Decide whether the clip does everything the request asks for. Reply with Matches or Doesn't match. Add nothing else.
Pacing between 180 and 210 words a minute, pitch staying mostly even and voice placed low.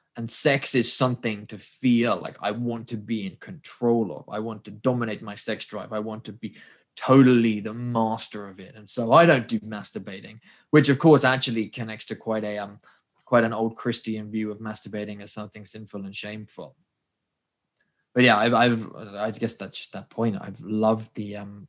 Matches